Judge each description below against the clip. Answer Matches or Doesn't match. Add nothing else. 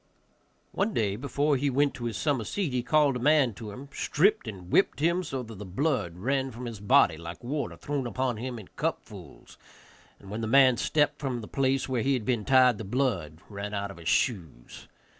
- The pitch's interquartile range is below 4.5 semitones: Doesn't match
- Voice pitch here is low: Matches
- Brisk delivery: Matches